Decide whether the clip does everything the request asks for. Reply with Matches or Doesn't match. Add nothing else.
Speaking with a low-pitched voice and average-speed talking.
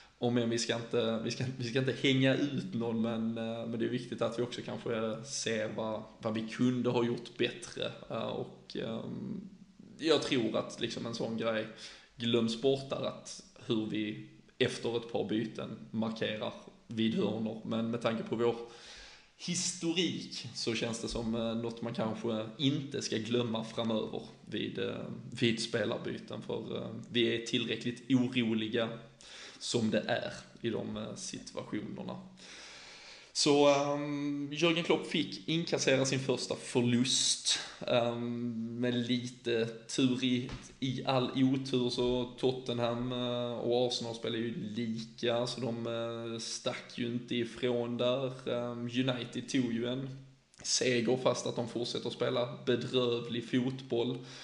Matches